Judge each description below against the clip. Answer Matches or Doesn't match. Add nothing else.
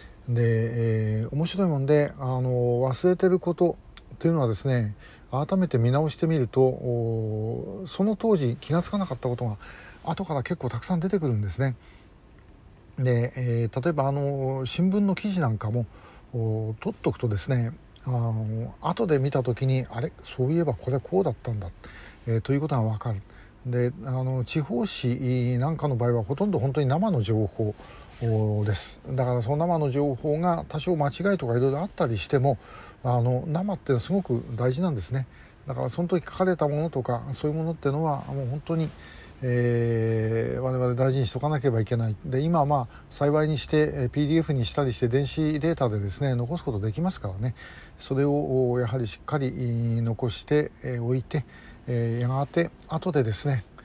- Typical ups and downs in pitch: Matches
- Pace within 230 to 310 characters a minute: Doesn't match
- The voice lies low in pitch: Matches